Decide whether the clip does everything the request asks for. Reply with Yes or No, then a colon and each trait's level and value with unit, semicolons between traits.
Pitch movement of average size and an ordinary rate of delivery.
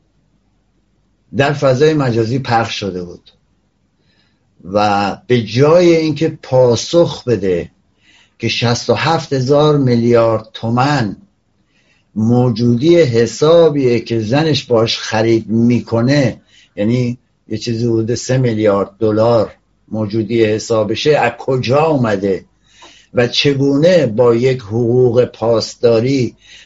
No: average, 3.3 semitones; slow, 95 wpm